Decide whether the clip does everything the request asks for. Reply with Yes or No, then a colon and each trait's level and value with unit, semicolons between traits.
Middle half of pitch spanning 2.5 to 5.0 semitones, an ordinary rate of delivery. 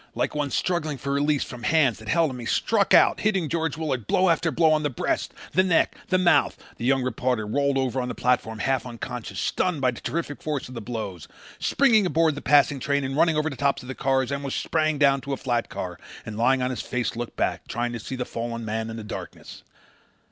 No: average, 4.3 semitones; fast, 235 wpm